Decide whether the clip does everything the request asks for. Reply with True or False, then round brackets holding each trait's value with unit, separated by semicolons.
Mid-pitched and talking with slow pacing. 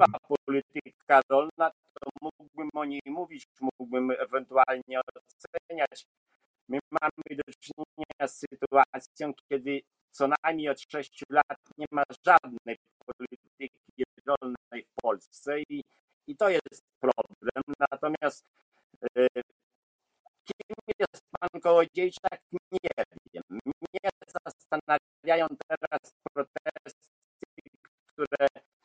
True (145 Hz; 100 wpm)